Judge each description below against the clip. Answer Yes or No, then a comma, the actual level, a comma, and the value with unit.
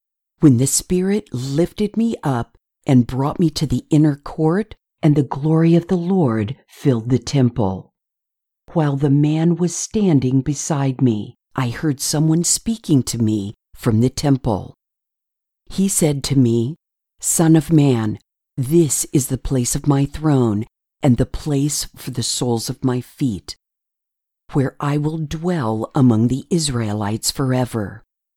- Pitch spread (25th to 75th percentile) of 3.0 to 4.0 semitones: No, average, 4.4 semitones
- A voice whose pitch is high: No, medium, 140 Hz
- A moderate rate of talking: Yes, average, 145 wpm